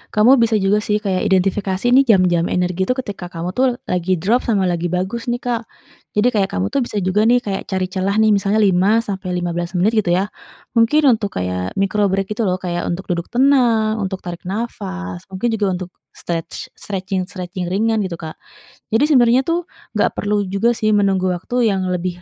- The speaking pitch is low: No, high, 195 Hz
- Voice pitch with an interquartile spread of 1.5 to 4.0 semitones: Yes, average, 3.5 semitones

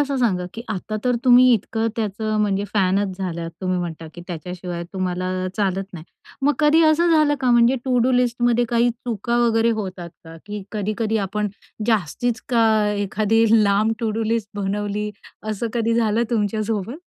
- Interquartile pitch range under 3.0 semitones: No, average, 3.6 semitones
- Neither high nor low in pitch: No, high, 215 Hz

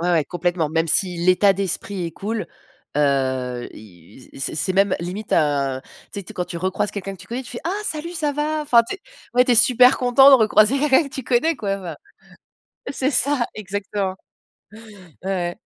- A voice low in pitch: No, high, 195 Hz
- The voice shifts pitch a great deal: Yes, wide, 6.7 semitones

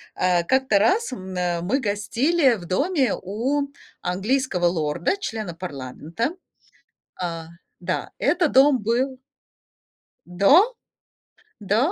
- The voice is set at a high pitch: Yes, high, 215 Hz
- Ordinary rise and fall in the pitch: No, wide, 7.3 semitones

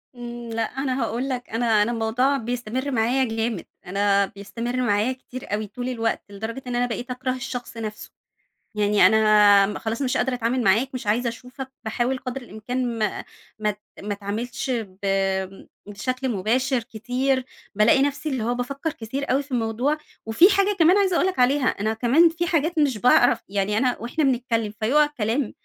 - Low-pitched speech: No, high, 240 Hz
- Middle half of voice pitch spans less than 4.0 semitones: Yes, average, 3.2 semitones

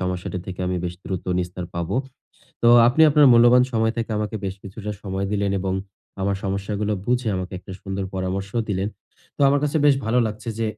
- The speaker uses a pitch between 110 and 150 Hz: No, low, 100 Hz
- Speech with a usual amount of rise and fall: Yes, average, 3.4 semitones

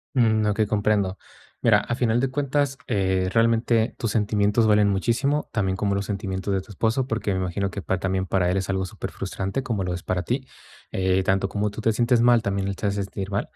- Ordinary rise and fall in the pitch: Yes, average, 3.1 semitones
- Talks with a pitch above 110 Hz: No, low, 100 Hz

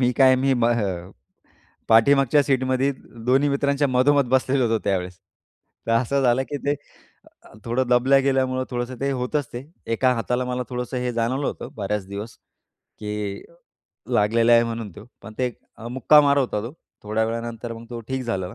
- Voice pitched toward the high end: No, low, 125 Hz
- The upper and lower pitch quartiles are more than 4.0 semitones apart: No, narrow, 2.6 semitones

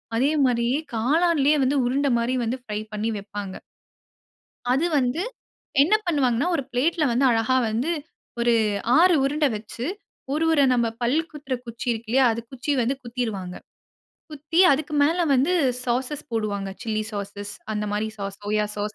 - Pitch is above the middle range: Yes, high, 245 Hz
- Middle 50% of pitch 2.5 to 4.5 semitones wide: No, average, 4.9 semitones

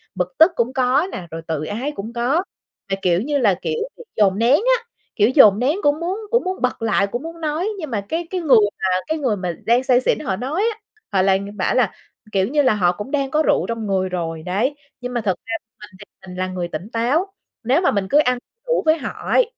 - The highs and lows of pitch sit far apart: Yes, wide, 7.4 semitones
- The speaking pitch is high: Yes, high, 240 Hz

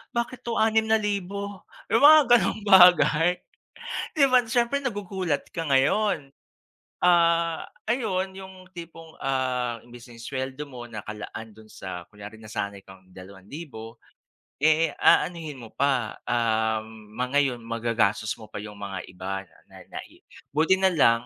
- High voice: No, medium, 140 Hz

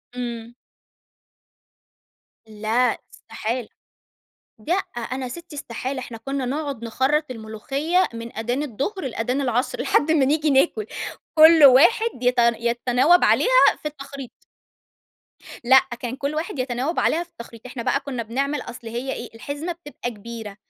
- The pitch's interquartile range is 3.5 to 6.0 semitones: Yes, average, 4.0 semitones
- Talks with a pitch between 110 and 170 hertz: No, very high, 260 Hz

